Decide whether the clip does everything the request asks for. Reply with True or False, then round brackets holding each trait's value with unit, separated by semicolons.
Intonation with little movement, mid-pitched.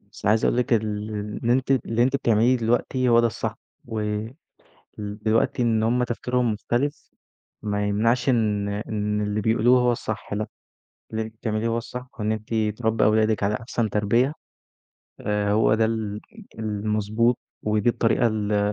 False (2.1 semitones; 110 Hz)